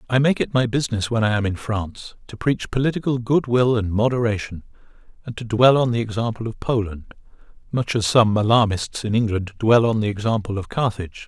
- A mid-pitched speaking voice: No, low, 115 Hz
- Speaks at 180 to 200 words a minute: Yes, average, 195 wpm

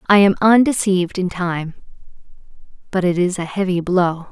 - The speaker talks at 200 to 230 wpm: No, average, 155 wpm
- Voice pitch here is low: No, medium, 185 Hz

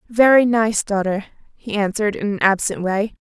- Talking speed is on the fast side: No, average, 165 wpm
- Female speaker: Yes, female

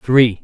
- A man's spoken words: Yes, male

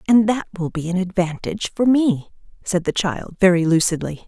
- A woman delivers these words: Yes, female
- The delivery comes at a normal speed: Yes, average, 180 wpm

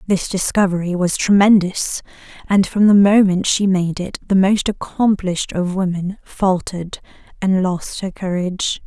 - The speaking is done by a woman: Yes, female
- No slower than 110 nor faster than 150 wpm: Yes, average, 140 wpm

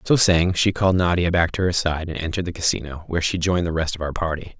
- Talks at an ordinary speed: No, fast, 275 wpm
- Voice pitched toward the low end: Yes, very low, 85 Hz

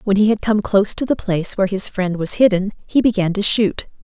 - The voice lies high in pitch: Yes, high, 200 Hz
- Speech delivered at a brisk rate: Yes, fast, 250 wpm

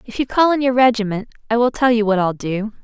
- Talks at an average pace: No, fast, 275 wpm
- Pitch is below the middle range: No, high, 230 Hz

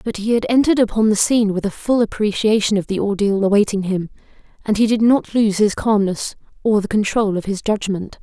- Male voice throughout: No, female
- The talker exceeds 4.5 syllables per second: Yes, 5.7 syllables/s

